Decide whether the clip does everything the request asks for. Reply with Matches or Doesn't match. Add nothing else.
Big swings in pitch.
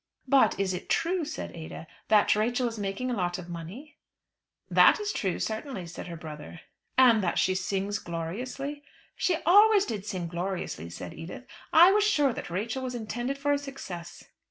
Matches